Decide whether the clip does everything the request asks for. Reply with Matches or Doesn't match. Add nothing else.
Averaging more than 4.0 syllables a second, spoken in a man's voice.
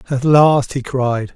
Doesn't match